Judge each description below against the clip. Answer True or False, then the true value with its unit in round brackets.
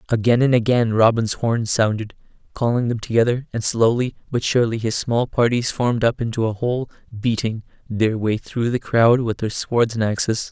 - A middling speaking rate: True (185 wpm)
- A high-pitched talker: False (115 Hz)